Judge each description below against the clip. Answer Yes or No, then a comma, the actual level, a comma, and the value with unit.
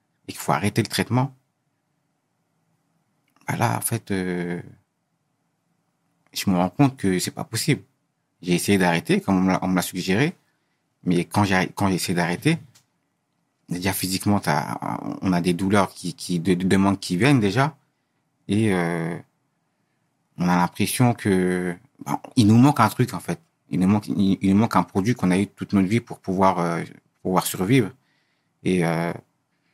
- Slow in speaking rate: No, average, 160 wpm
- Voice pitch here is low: Yes, low, 100 Hz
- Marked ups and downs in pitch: Yes, wide, 7.8 semitones